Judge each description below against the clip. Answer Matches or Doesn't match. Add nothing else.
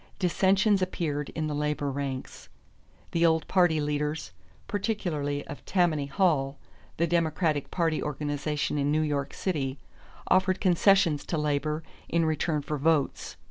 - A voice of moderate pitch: Matches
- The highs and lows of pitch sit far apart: Doesn't match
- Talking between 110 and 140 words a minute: Matches